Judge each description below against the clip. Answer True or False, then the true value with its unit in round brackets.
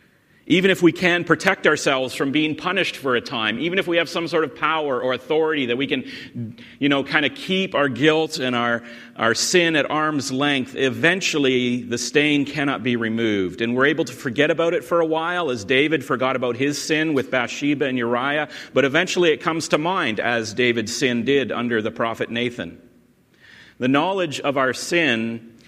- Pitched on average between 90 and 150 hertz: True (140 Hz)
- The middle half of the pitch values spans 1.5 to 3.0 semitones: False (4.9 semitones)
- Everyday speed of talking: True (195 wpm)